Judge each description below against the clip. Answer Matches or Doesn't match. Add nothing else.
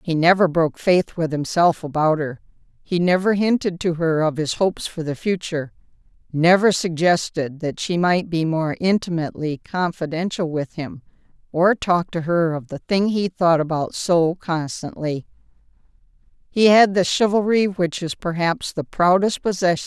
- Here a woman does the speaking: Matches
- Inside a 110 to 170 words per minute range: Matches